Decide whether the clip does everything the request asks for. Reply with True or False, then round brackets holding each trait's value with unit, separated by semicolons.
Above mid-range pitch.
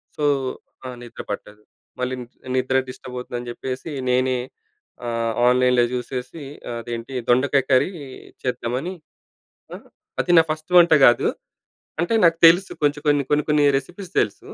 False (130 Hz)